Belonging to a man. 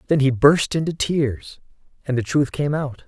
Yes: male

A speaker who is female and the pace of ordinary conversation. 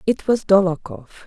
Yes: female; average, 145 wpm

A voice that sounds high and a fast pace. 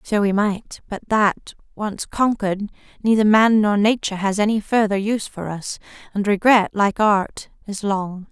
No: high, 205 Hz; average, 165 wpm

